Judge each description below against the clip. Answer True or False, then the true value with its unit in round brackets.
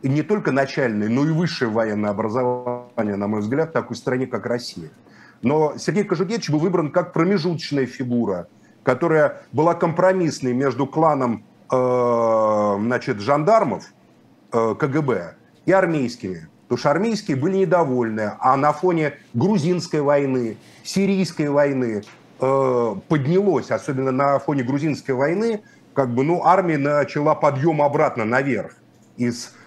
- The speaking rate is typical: True (125 wpm)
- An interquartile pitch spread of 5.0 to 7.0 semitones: True (5.3 semitones)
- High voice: False (140 Hz)